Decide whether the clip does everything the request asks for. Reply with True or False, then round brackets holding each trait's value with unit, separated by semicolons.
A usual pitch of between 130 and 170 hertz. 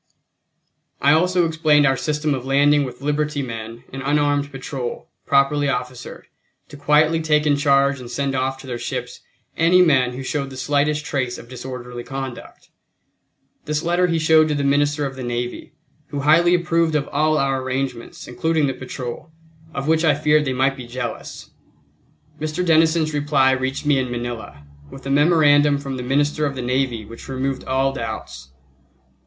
True (140 Hz)